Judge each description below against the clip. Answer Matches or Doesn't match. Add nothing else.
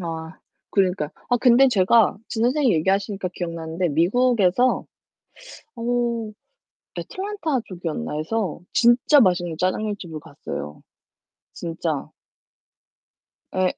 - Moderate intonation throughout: Doesn't match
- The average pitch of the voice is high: Matches